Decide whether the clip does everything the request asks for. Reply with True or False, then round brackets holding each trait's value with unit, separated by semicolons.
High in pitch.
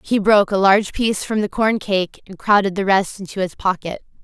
True (200 Hz)